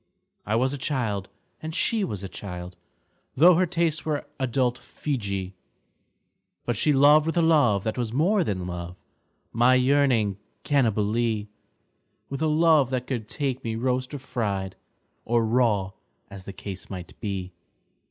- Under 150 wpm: No, average, 160 wpm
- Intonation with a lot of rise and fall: Yes, wide, 6.1 semitones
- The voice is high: No, low, 120 Hz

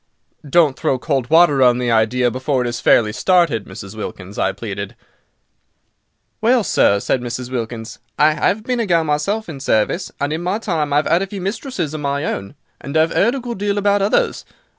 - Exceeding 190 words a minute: Yes, average, 200 wpm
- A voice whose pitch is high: No, medium, 150 Hz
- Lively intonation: Yes, wide, 7.6 semitones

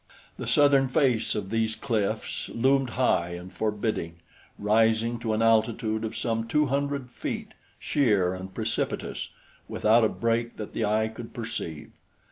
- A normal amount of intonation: No, narrow, 2.0 semitones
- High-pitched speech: No, low, 115 Hz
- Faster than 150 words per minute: No, average, 145 wpm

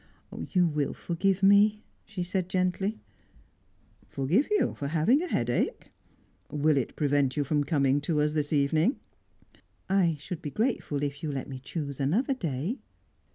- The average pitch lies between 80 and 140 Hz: No, medium, 155 Hz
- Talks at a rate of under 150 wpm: No, average, 155 wpm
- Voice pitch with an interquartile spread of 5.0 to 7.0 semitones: Yes, average, 5.3 semitones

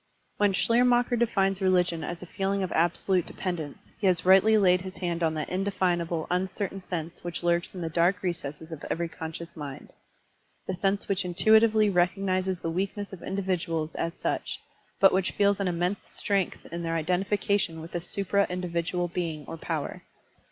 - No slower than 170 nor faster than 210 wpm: Yes, average, 175 wpm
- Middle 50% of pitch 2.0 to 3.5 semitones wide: Yes, narrow, 2.5 semitones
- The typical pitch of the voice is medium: Yes, medium, 180 Hz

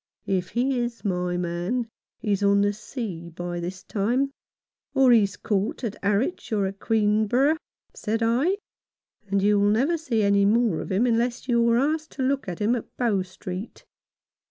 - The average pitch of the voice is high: Yes, high, 215 Hz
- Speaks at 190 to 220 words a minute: No, average, 175 wpm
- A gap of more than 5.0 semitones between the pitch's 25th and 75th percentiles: No, average, 3.8 semitones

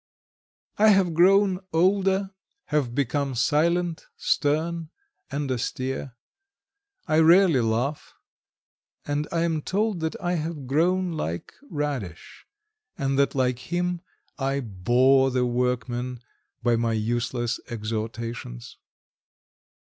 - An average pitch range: No, wide, 5.8 semitones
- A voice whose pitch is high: No, medium, 140 Hz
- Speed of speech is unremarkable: No, slow, 105 wpm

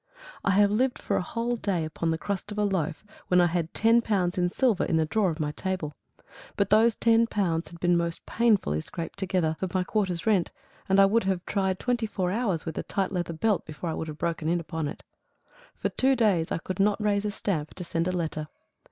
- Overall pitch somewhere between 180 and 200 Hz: Yes, medium, 185 Hz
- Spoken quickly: Yes, fast, 235 wpm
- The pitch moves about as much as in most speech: Yes, average, 4.0 semitones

